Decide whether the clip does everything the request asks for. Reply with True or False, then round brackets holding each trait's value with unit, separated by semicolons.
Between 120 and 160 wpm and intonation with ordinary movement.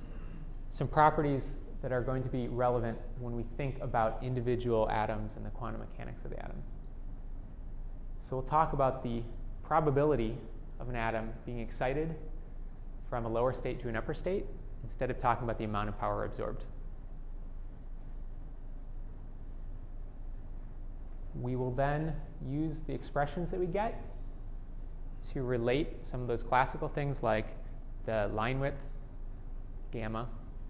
True (135 wpm; 3.7 semitones)